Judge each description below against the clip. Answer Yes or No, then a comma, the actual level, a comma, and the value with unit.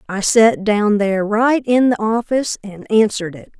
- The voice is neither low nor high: No, high, 215 Hz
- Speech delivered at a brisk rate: No, average, 185 wpm